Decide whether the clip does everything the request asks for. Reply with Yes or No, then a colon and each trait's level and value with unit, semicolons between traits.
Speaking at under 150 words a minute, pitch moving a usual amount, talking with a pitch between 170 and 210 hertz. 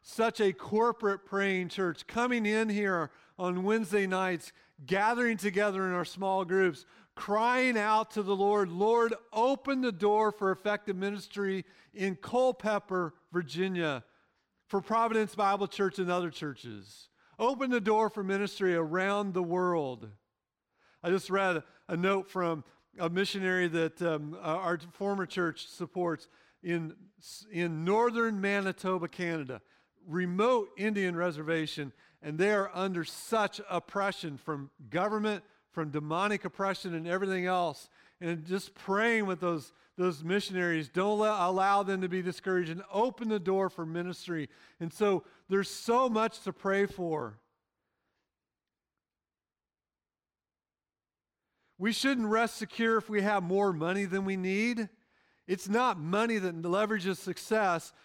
Yes: slow, 135 wpm; average, 3.3 semitones; high, 190 Hz